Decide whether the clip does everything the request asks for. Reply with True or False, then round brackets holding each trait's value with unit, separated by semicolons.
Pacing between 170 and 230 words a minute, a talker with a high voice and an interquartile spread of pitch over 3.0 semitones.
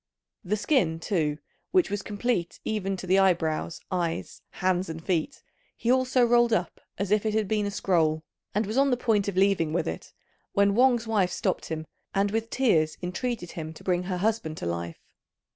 True (195 wpm; 195 Hz; 4.9 semitones)